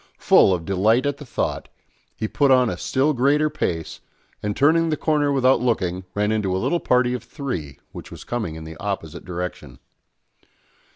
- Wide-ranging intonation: Yes, wide, 7.4 semitones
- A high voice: No, low, 115 Hz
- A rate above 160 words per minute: Yes, average, 180 wpm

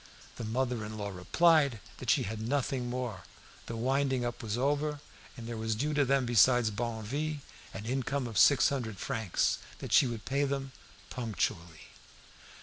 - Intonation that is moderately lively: Yes, average, 3.7 semitones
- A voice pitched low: Yes, low, 120 Hz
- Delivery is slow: No, average, 165 wpm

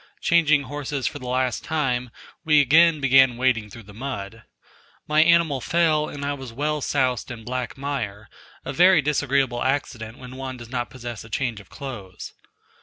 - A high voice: No, low, 130 Hz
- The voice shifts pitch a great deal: No, average, 3.3 semitones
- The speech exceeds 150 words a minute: Yes, average, 175 wpm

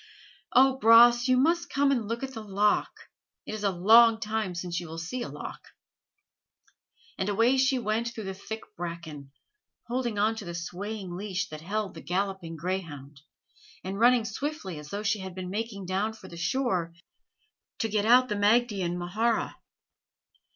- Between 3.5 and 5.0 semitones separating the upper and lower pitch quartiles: Yes, average, 4.5 semitones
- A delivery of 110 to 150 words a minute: No, average, 170 wpm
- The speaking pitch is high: Yes, high, 205 Hz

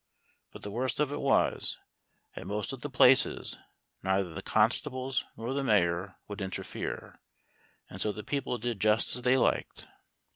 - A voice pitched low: Yes, low, 115 Hz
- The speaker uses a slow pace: No, average, 160 wpm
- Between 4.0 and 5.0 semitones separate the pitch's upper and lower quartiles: Yes, average, 4.3 semitones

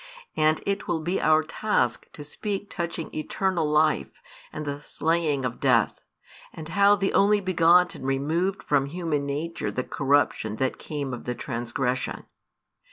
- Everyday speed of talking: Yes, average, 155 wpm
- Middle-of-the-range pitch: Yes, medium, 155 Hz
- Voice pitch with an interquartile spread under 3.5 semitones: No, average, 4.2 semitones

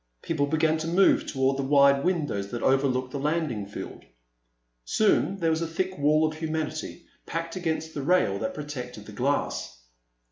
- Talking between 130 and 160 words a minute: No, average, 170 wpm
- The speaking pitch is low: No, medium, 150 Hz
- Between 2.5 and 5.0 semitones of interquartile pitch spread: Yes, average, 3.5 semitones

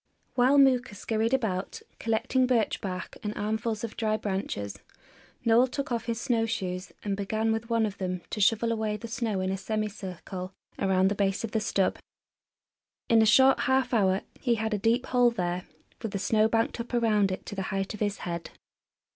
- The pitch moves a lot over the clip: No, average, 3.1 semitones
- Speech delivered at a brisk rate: No, average, 195 wpm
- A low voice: No, high, 215 Hz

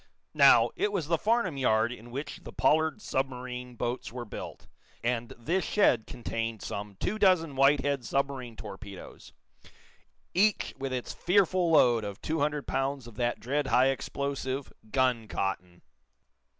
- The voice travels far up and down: No, average, 4.1 semitones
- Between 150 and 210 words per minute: No, average, 140 wpm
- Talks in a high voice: No, low, 130 Hz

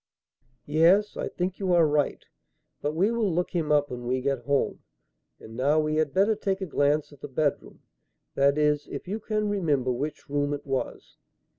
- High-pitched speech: No, medium, 150 Hz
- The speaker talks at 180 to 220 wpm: Yes, average, 190 wpm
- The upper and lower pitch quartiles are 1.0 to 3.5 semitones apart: No, average, 4.6 semitones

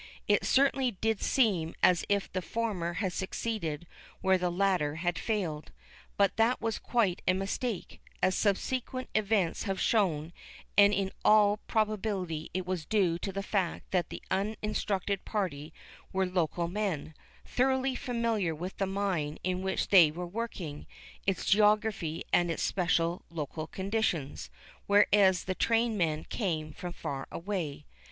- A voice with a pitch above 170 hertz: Yes, high, 190 Hz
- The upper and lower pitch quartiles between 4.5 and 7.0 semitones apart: No, average, 3.8 semitones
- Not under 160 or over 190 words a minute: No, average, 145 wpm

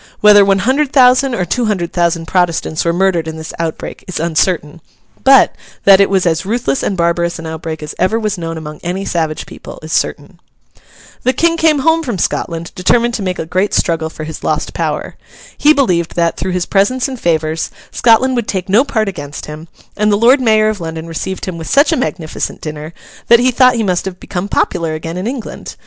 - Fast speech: Yes, fast, 210 wpm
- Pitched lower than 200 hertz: Yes, medium, 185 Hz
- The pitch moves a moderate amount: No, wide, 5.8 semitones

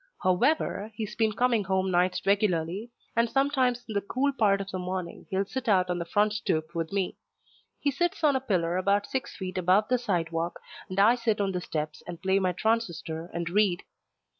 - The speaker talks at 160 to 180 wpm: No, average, 200 wpm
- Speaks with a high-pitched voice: Yes, high, 195 Hz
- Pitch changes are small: No, average, 4.2 semitones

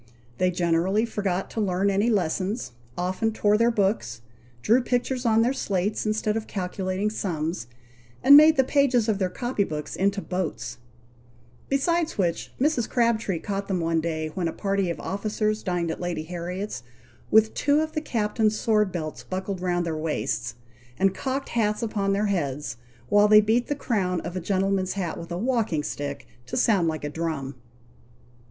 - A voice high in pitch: Yes, high, 195 Hz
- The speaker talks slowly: No, average, 175 wpm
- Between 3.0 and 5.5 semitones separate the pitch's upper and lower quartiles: Yes, average, 4.1 semitones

